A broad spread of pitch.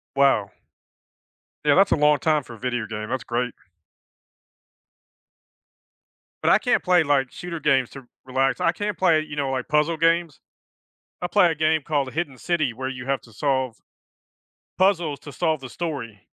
No: average, 4.1 semitones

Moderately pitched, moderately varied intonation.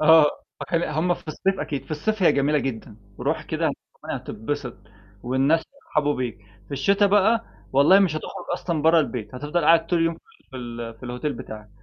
Yes: medium, 150 Hz; average, 4.8 semitones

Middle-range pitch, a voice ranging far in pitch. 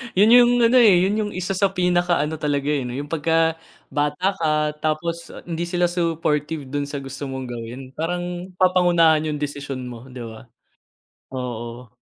No: medium, 155 Hz; average, 4.4 semitones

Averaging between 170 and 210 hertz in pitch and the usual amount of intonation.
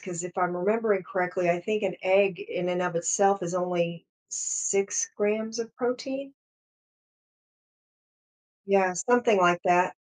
Yes: high, 190 Hz; average, 3.1 semitones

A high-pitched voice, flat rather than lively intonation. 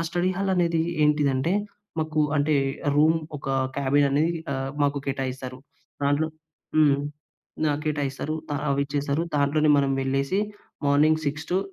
No: medium, 145 Hz; narrow, 2.1 semitones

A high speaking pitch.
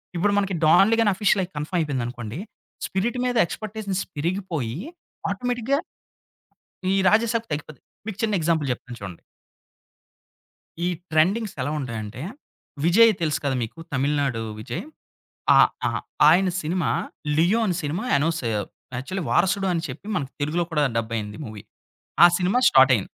No: medium, 165 Hz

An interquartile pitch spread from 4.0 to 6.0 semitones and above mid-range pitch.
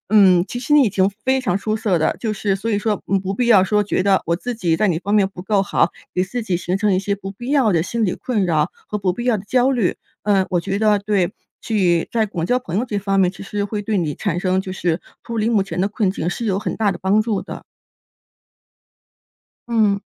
No: average, 2.7 semitones; high, 200 Hz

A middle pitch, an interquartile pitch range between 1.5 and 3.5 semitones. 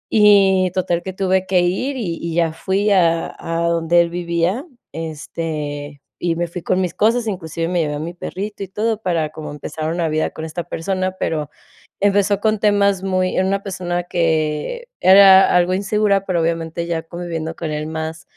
Yes: medium, 175 Hz; average, 2.9 semitones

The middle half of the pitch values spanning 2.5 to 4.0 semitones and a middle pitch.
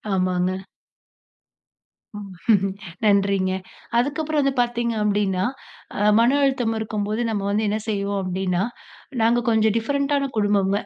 No: average, 3.4 semitones; high, 210 Hz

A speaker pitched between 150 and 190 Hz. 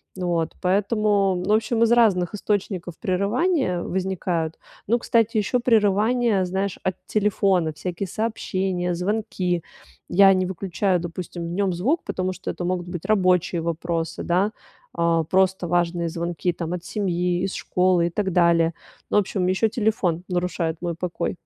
Yes: medium, 185 Hz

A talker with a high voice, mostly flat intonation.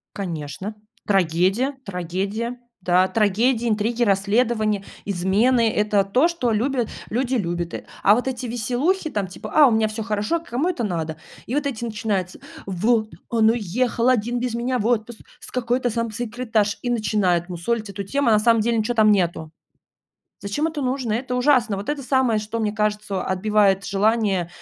No: high, 220 Hz; average, 3.5 semitones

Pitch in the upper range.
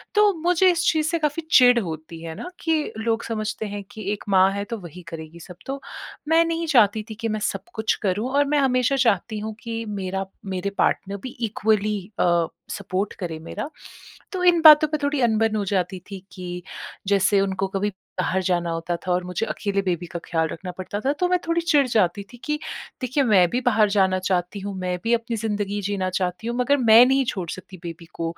Yes: high, 205 Hz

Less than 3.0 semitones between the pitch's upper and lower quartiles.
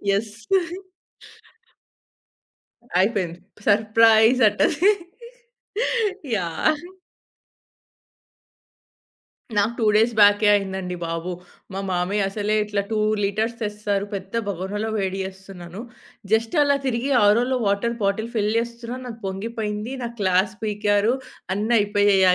Yes: narrow, 2.6 semitones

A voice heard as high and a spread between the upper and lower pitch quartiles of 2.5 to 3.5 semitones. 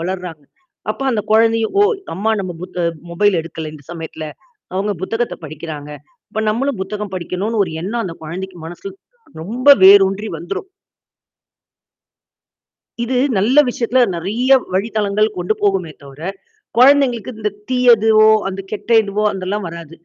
No: high, 200 Hz; average, 4.4 semitones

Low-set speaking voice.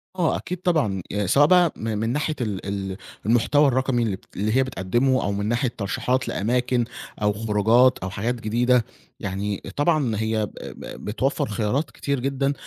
Yes: low, 120 Hz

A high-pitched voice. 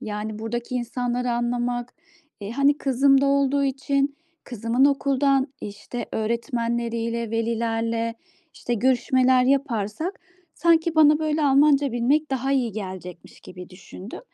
Yes: high, 245 Hz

